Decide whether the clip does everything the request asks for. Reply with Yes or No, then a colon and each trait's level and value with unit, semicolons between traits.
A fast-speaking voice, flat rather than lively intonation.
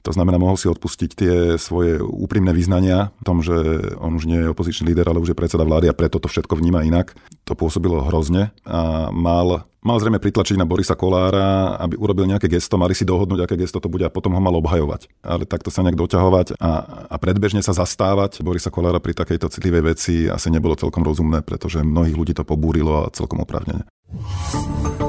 Yes: fast, 200 wpm; narrow, 2.2 semitones